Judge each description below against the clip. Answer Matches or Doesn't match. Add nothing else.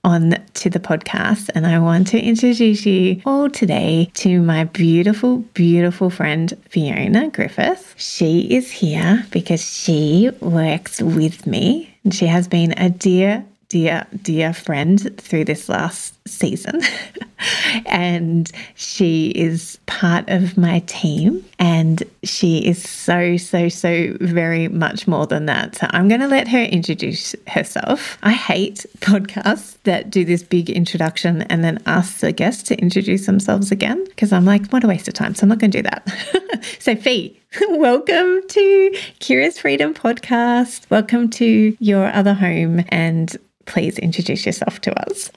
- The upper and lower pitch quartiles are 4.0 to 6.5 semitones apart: Matches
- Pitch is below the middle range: Doesn't match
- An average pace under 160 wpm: Matches